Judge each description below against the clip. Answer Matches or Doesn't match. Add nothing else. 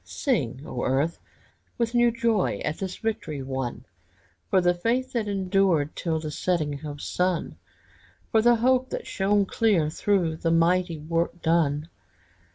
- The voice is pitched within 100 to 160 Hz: Doesn't match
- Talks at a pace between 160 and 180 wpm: Doesn't match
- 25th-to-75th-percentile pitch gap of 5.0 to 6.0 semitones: Matches